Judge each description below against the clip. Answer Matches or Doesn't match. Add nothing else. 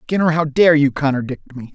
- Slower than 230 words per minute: Matches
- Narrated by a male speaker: Matches